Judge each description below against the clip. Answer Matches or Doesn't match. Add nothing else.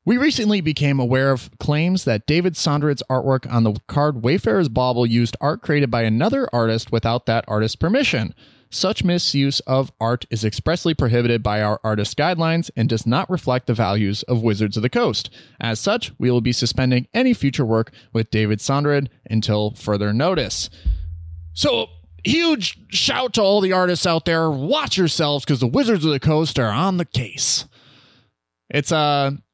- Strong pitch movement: Matches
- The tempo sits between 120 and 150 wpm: Doesn't match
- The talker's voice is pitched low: Matches